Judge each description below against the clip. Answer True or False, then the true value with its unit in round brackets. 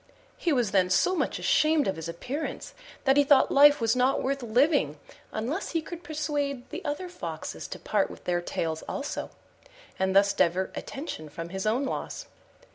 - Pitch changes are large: True (7.5 semitones)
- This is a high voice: True (255 Hz)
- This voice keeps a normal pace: True (180 wpm)